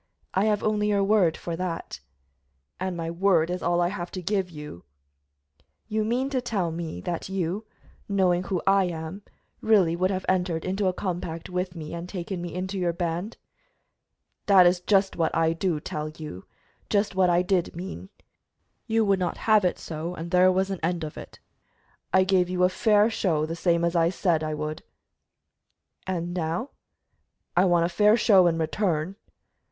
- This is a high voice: No, medium, 180 Hz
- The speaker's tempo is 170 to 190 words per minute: Yes, average, 185 wpm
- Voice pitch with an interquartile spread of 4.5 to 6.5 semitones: No, narrow, 2.5 semitones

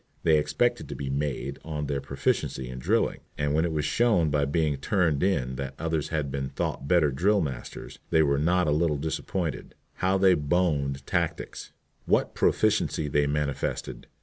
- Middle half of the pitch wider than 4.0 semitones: No, average, 3.3 semitones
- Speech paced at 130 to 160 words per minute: No, average, 175 wpm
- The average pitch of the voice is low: Yes, very low, 75 Hz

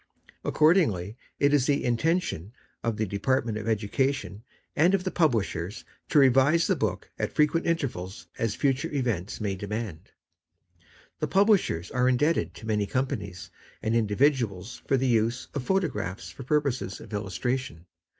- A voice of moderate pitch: No, low, 120 Hz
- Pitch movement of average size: No, wide, 5.8 semitones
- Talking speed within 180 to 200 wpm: No, average, 150 wpm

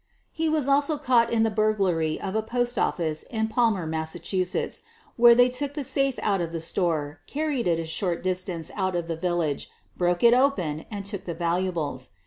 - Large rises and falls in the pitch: Yes, wide, 6.3 semitones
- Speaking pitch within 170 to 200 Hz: Yes, high, 190 Hz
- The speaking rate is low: No, average, 190 wpm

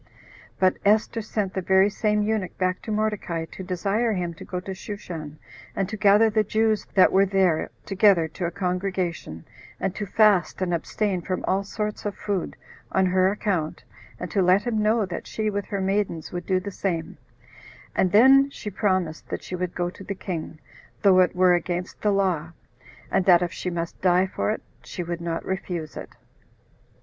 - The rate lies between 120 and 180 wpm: No, average, 190 wpm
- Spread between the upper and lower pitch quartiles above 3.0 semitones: No, narrow, 2.6 semitones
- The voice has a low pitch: No, high, 190 Hz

